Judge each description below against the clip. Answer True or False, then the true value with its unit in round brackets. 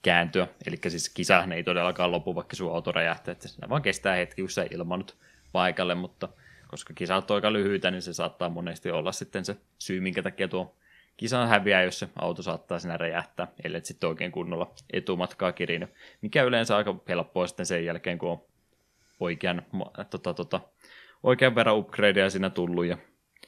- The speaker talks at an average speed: False (170 wpm)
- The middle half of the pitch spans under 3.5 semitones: True (2.5 semitones)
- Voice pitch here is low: True (90 Hz)